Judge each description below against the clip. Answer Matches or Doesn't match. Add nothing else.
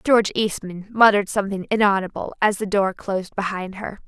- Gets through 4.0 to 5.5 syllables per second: Doesn't match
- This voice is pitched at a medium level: Doesn't match